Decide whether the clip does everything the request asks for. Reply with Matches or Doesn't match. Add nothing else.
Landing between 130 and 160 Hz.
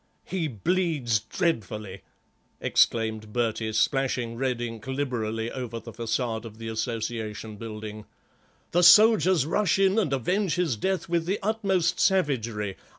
Doesn't match